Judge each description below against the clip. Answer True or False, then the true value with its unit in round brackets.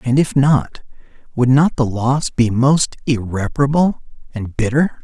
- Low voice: True (130 Hz)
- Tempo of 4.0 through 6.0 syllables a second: True (4.3 syllables/s)